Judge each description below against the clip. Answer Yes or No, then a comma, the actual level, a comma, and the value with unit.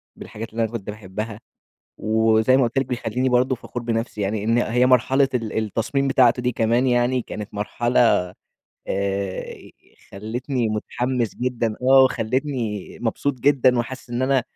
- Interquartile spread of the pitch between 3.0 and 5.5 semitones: No, narrow, 2.6 semitones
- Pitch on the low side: Yes, low, 120 Hz